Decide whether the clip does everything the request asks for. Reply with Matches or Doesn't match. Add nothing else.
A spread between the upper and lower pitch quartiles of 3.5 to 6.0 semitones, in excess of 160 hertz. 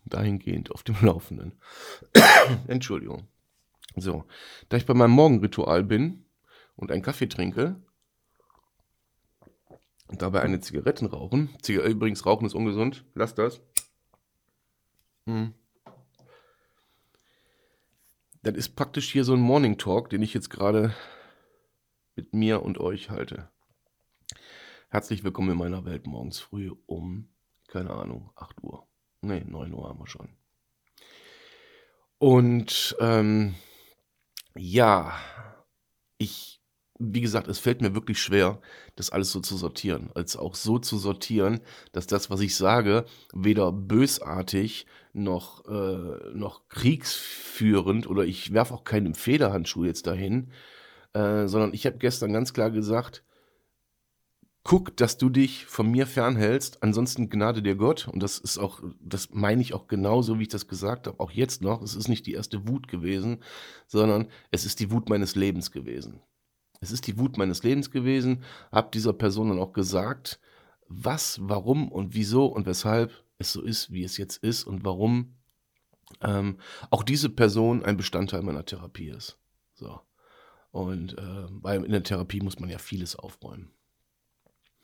Doesn't match